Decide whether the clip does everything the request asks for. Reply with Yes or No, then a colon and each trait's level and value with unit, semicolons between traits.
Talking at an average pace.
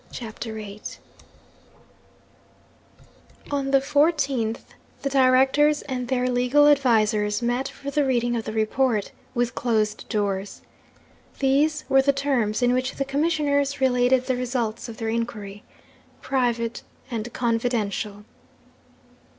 No: slow, 120 wpm